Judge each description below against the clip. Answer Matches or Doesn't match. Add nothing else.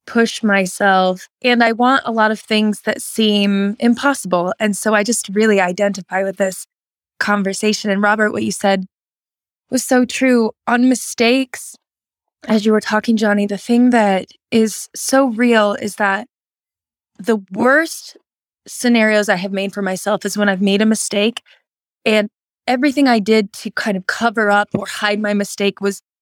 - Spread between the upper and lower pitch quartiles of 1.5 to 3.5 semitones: Matches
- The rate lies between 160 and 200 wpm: Matches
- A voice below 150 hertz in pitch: Doesn't match